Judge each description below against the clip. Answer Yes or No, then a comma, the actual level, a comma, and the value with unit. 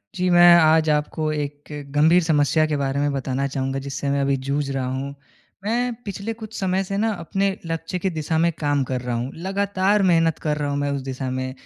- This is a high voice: No, medium, 155 Hz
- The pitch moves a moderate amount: Yes, average, 4.6 semitones